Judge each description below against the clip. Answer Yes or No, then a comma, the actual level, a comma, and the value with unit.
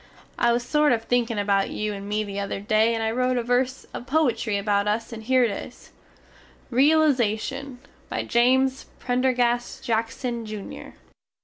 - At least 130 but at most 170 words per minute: Yes, average, 165 wpm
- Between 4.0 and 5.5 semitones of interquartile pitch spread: No, average, 3.0 semitones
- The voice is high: Yes, high, 235 Hz